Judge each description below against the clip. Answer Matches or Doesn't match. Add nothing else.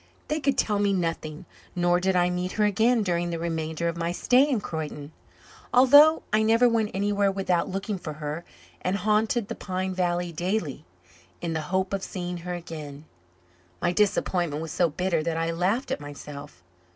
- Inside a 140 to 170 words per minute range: Doesn't match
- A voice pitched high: Doesn't match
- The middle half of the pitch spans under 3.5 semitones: Doesn't match